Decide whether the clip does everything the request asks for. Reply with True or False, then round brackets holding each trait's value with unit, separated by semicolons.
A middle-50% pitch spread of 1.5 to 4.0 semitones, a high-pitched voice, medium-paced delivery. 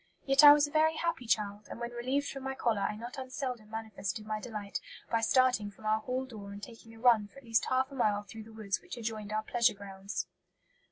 False (3.4 semitones; 225 Hz; 235 wpm)